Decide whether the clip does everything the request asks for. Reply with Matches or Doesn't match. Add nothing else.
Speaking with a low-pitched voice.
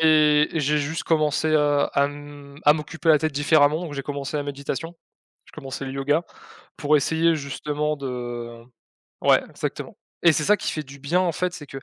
Doesn't match